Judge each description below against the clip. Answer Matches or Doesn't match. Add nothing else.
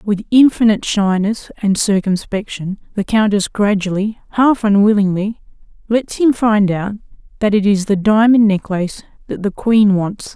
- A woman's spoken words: Matches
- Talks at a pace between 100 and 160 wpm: Matches